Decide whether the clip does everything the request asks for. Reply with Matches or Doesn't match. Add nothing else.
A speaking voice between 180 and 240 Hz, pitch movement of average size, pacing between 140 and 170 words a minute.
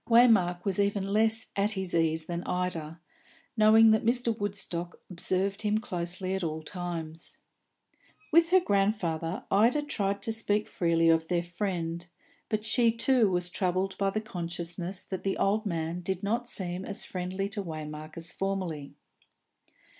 Matches